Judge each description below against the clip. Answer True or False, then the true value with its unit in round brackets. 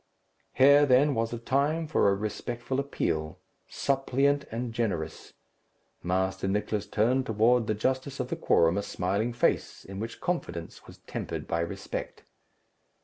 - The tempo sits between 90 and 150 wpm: True (145 wpm)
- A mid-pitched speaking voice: False (115 Hz)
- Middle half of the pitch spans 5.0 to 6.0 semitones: True (5.3 semitones)